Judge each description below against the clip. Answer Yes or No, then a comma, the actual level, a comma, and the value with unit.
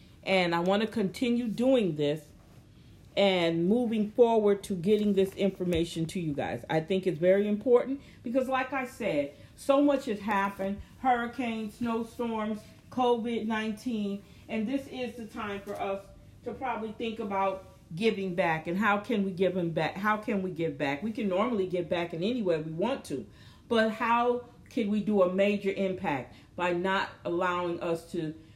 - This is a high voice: Yes, high, 205 Hz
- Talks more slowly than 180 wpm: Yes, average, 170 wpm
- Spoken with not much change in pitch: No, average, 4.3 semitones